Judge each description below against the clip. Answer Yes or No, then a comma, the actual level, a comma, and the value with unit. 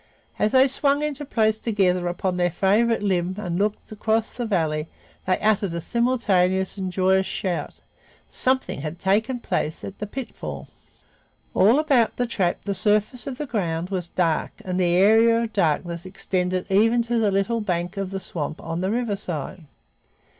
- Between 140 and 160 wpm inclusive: No, average, 170 wpm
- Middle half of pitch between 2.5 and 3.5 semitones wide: No, average, 4.1 semitones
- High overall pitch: Yes, high, 195 Hz